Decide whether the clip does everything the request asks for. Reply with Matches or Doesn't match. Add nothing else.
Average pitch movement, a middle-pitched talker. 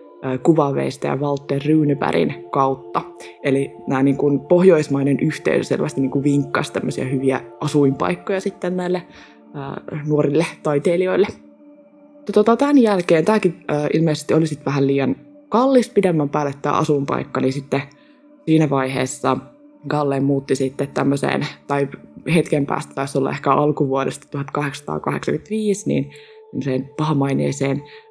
Matches